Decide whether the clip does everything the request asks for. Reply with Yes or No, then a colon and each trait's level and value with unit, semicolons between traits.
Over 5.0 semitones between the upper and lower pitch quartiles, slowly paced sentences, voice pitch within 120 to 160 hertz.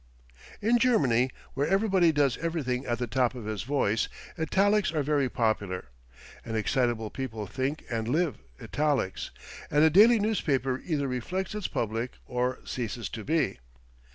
No: wide, 5.5 semitones; average, 150 wpm; low, 135 Hz